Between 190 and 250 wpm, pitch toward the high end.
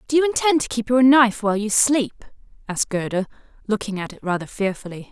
Yes: average, 200 wpm; high, 225 Hz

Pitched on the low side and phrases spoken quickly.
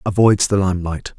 No: very low, 95 Hz; average, 150 wpm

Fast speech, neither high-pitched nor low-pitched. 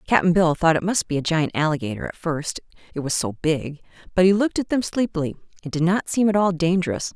Yes: fast, 235 wpm; medium, 170 Hz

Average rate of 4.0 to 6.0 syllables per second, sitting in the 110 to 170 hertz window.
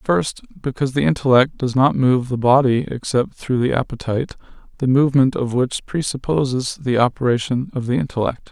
Yes: 5.3 syllables/s; low, 130 Hz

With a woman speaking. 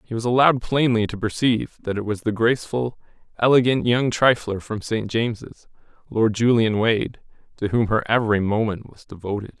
No: male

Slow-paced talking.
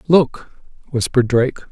Yes: slow, 105 wpm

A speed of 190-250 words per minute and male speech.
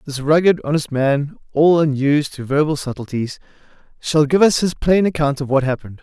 No: average, 180 wpm; male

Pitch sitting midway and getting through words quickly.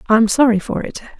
No: high, 230 Hz; fast, 250 wpm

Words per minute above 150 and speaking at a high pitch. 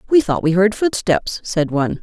Yes: fast, 205 wpm; high, 195 Hz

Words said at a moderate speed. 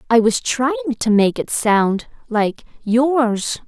No: slow, 130 wpm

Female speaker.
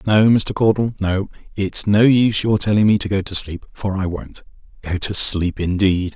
No: male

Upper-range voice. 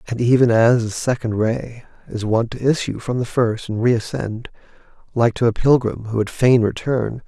No: low, 120 Hz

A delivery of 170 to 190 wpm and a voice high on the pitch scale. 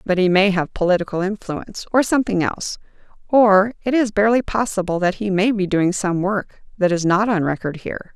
No: average, 200 wpm; high, 195 Hz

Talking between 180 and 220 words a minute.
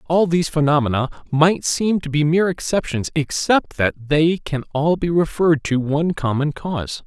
No: average, 170 wpm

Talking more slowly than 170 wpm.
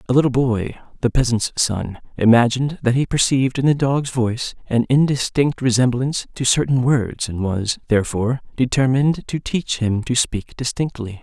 Yes: average, 160 wpm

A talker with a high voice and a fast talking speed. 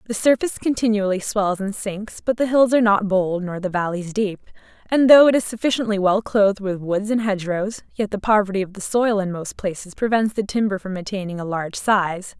Yes: high, 205 Hz; fast, 215 wpm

